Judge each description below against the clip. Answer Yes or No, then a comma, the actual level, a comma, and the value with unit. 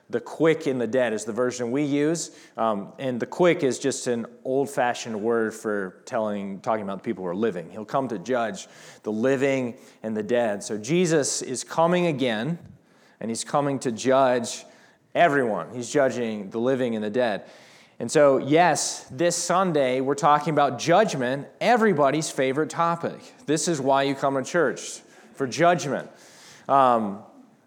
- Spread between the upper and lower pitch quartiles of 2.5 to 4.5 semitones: No, average, 5.1 semitones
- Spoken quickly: No, average, 165 wpm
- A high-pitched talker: No, low, 135 Hz